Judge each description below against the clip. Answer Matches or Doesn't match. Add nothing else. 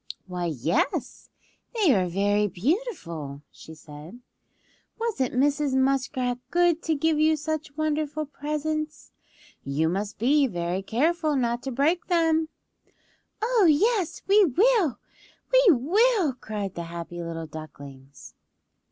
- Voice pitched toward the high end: Matches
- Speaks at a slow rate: Matches